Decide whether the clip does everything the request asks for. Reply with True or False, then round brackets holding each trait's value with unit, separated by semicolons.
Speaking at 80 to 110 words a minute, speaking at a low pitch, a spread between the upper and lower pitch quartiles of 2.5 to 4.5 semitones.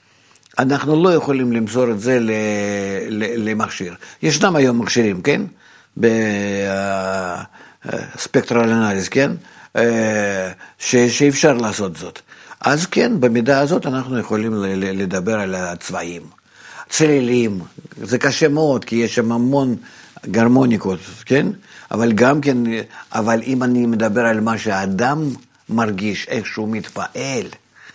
True (105 wpm; 115 Hz; 3.7 semitones)